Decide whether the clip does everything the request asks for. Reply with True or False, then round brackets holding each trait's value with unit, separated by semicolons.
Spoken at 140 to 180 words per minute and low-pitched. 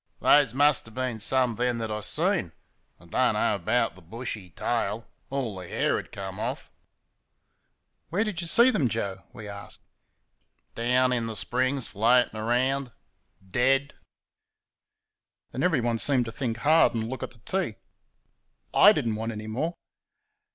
True (155 wpm; 120 Hz)